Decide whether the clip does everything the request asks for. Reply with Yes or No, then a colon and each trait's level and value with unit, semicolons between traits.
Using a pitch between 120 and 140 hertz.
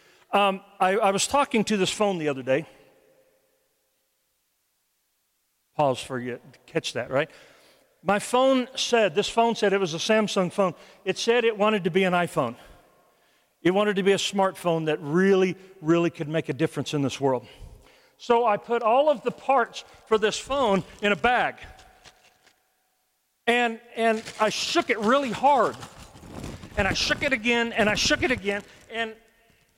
No: high, 205 Hz